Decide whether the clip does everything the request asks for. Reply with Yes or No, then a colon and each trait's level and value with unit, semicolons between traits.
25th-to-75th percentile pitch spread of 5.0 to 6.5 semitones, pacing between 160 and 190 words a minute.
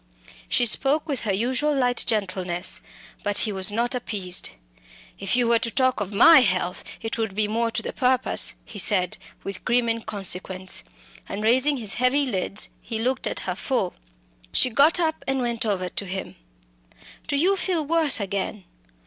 No: average, 4.6 semitones; average, 175 wpm